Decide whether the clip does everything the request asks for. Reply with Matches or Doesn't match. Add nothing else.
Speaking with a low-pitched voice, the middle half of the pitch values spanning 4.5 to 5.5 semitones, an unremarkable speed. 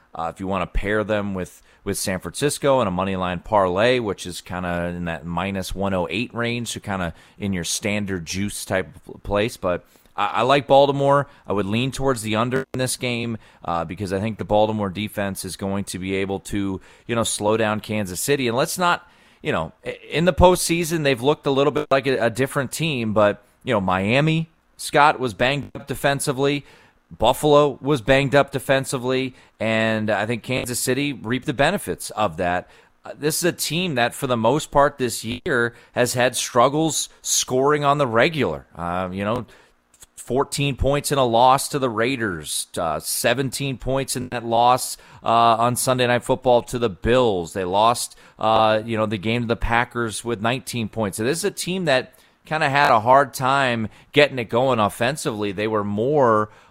Matches